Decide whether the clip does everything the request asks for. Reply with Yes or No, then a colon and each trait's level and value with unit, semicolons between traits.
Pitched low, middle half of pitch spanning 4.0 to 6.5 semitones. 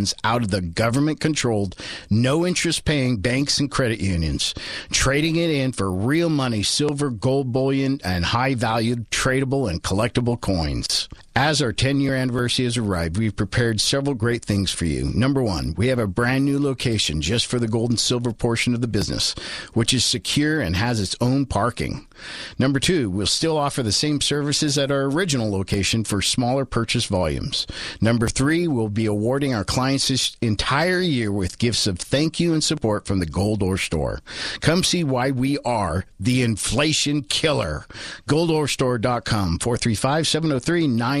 Yes: low, 120 Hz; average, 4.9 semitones